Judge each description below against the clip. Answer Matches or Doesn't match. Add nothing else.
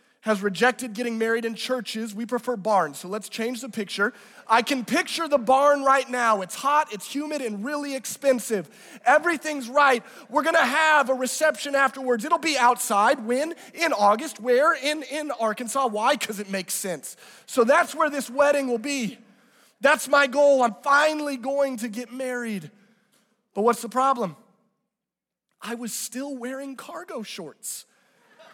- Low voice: Doesn't match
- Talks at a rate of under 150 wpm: Doesn't match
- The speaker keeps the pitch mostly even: Doesn't match